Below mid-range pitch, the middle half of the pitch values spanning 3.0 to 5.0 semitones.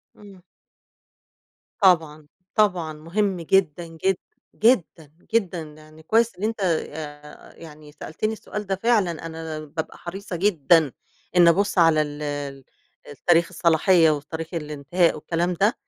No: medium, 170 Hz; average, 3.8 semitones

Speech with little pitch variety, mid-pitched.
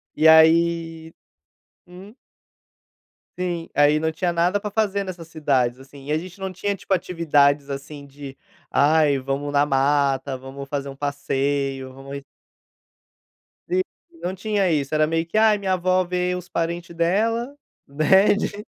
No: average, 4.4 semitones; medium, 160 Hz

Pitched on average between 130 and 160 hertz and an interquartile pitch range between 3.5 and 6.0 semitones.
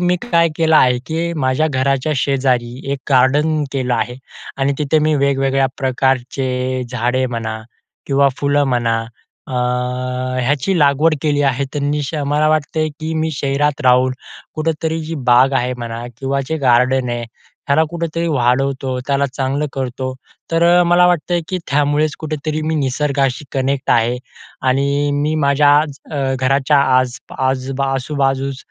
No: medium, 140 Hz; average, 2.8 semitones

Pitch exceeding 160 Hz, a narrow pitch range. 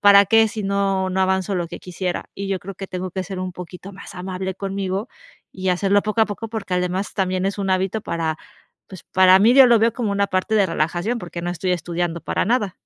Yes: high, 190 Hz; narrow, 1.8 semitones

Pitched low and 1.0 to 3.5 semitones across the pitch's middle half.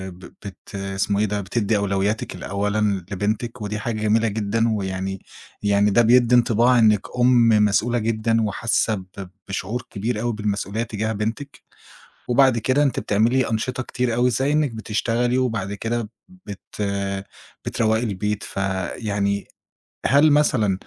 Yes: low, 110 Hz; average, 2.9 semitones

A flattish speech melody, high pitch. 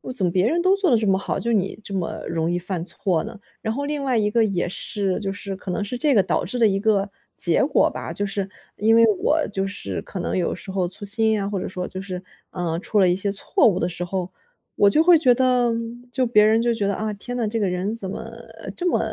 No: average, 3.5 semitones; high, 205 Hz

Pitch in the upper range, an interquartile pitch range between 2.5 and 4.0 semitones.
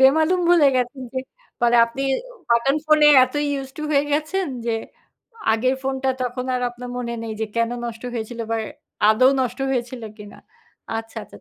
Yes: very high, 255 Hz; average, 2.9 semitones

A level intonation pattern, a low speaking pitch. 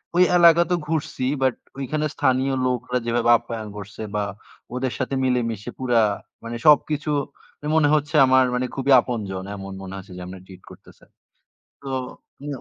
No: average, 3.8 semitones; low, 125 Hz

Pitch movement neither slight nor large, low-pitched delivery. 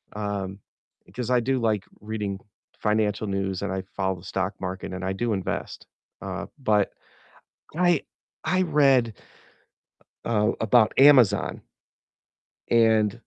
Yes: average, 3.7 semitones; low, 105 Hz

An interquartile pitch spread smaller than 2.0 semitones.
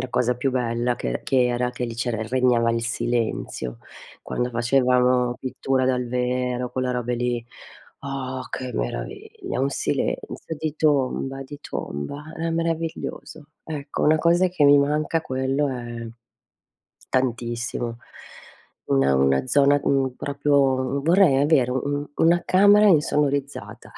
No: average, 2.8 semitones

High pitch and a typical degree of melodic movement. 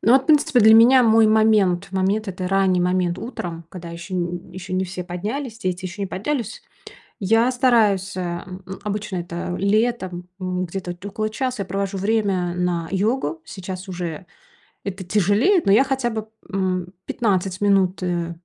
Yes: high, 195 Hz; average, 3.4 semitones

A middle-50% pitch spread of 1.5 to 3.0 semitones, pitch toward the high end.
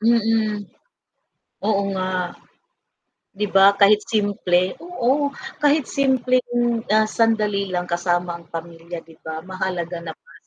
No: average, 4.4 semitones; high, 200 Hz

